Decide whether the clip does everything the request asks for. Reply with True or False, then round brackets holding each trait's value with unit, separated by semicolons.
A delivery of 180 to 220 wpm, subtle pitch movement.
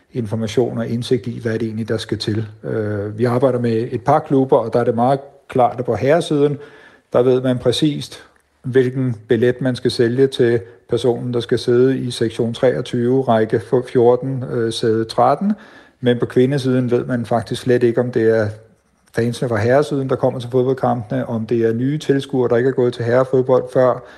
True (190 wpm; 1.8 semitones)